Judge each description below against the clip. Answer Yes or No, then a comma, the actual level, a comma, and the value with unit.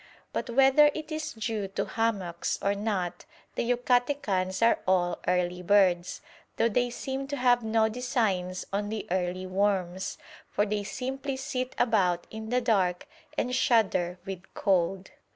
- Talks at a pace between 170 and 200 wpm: No, average, 150 wpm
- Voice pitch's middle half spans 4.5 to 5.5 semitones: Yes, average, 4.9 semitones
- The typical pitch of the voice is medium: No, high, 210 Hz